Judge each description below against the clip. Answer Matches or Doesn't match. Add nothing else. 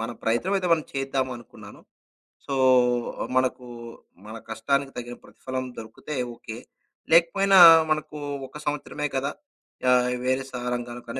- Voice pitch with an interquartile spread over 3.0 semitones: Matches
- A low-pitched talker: Matches